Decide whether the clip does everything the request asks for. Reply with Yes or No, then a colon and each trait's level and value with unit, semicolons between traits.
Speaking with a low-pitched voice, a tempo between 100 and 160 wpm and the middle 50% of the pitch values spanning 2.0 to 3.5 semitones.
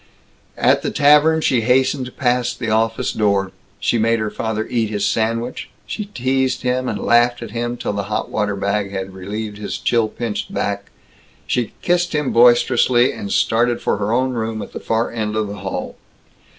No: low, 115 Hz; average, 185 wpm; average, 2.9 semitones